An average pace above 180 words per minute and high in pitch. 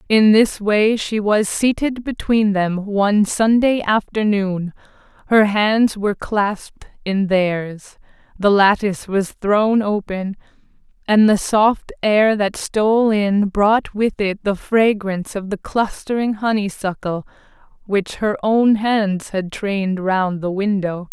No: slow, 135 wpm; high, 205 Hz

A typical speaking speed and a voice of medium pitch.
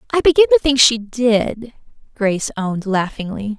No: average, 150 wpm; high, 235 Hz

